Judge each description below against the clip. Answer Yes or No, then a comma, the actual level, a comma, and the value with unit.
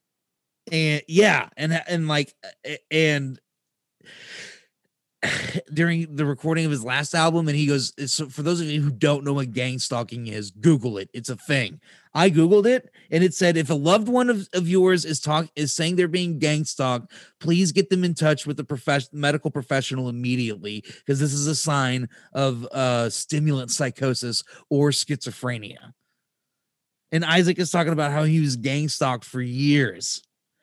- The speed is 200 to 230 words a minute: No, average, 170 wpm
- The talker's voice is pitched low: No, medium, 150 Hz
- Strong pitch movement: No, average, 3.9 semitones